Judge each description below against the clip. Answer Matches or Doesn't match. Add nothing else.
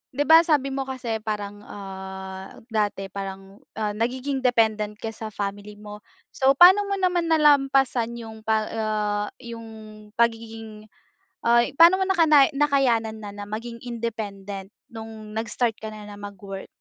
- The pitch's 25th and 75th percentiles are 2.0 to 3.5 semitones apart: Doesn't match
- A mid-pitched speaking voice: Doesn't match